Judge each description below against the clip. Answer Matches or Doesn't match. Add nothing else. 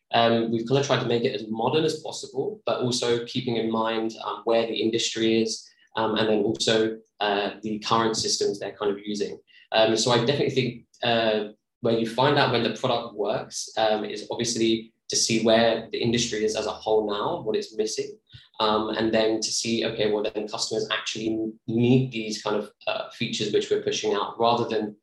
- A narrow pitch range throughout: Matches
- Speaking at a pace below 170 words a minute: Doesn't match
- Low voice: Matches